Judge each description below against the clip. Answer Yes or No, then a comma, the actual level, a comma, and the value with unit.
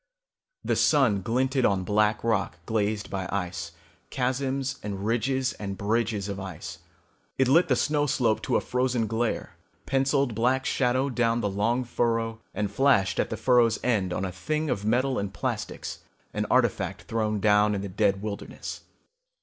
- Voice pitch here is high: No, low, 115 Hz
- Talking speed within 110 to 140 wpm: No, average, 165 wpm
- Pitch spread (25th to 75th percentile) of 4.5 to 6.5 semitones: No, average, 4.1 semitones